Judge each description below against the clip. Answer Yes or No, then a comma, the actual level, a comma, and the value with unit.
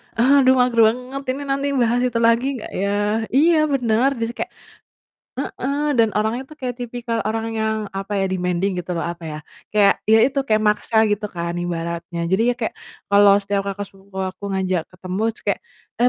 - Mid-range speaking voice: No, high, 220 Hz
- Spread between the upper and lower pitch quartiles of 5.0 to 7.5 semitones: No, average, 4.3 semitones